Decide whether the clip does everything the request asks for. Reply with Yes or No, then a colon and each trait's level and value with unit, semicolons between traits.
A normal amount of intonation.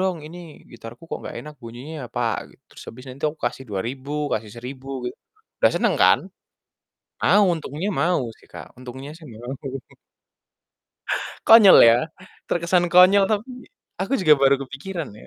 No: wide, 6.2 semitones